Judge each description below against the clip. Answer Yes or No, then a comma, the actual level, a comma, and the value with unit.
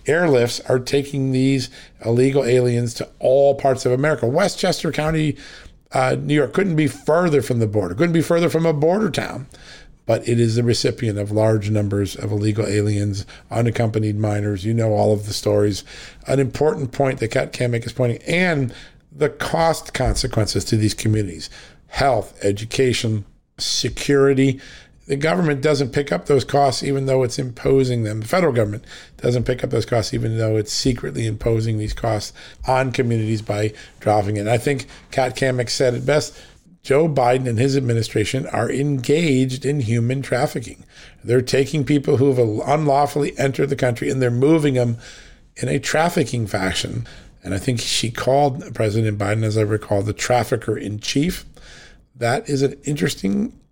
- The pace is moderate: Yes, average, 170 wpm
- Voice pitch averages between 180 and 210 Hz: No, low, 125 Hz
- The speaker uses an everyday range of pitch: Yes, average, 4.2 semitones